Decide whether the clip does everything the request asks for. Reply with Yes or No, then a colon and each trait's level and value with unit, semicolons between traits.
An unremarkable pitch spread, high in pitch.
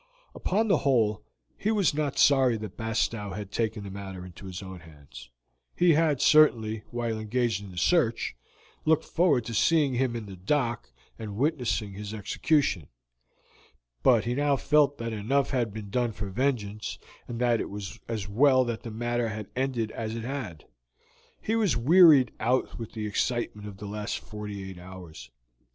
No: average, 4.6 semitones; low, 115 Hz